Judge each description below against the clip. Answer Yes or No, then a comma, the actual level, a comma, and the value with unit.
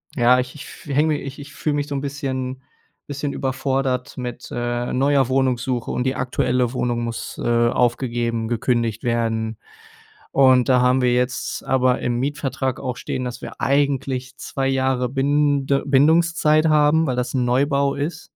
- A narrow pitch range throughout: Yes, narrow, 2.2 semitones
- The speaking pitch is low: Yes, low, 130 Hz